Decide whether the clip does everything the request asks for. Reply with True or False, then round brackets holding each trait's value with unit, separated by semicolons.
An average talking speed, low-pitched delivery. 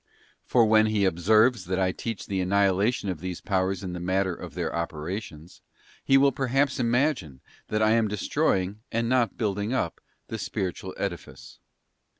True (160 wpm; 100 Hz)